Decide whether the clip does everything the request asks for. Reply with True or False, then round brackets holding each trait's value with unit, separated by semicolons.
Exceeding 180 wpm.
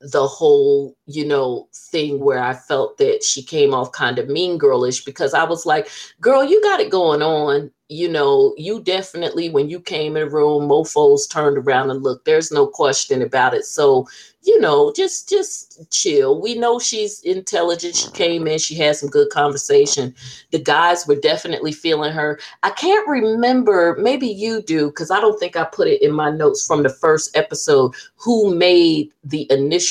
True (190 wpm)